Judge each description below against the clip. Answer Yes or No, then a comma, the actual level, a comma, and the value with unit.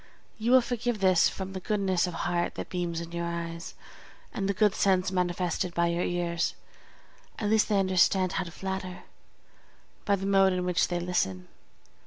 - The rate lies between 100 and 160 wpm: No, average, 180 wpm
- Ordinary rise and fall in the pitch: No, narrow, 2.1 semitones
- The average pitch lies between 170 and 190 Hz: Yes, medium, 185 Hz